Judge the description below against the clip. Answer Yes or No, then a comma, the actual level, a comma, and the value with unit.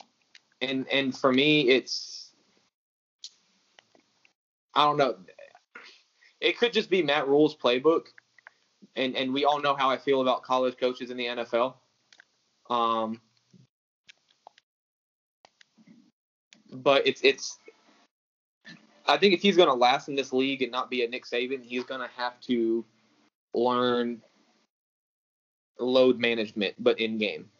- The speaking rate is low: Yes, slow, 125 wpm